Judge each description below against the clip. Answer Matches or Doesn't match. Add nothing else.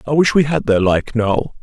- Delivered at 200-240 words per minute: Doesn't match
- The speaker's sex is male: Matches